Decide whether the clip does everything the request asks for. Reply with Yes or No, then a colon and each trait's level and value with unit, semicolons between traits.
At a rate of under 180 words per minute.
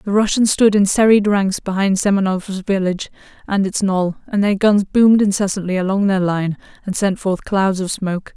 No: average, 185 wpm